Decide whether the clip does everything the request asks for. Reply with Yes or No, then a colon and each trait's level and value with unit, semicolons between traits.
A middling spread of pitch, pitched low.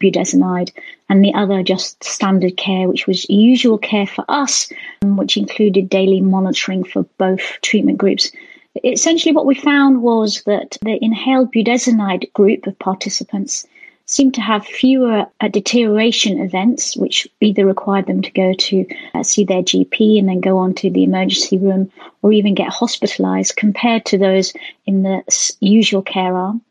No: average, 3.6 semitones; high, 200 Hz